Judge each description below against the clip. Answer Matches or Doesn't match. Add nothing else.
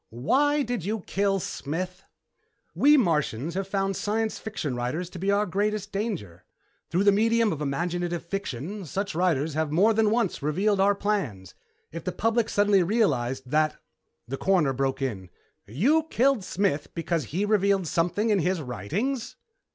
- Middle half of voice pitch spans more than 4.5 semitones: Matches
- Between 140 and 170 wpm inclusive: Matches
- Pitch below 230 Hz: Matches